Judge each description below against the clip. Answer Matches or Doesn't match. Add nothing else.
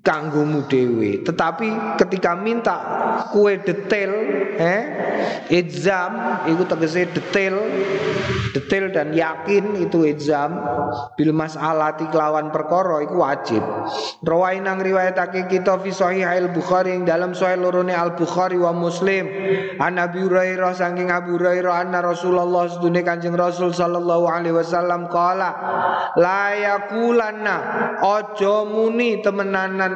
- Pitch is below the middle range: Doesn't match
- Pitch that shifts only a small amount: Matches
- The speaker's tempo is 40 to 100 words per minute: Doesn't match